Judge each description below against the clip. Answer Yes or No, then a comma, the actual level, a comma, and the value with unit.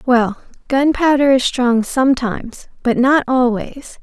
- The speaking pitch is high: Yes, very high, 255 Hz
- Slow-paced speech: Yes, slow, 120 wpm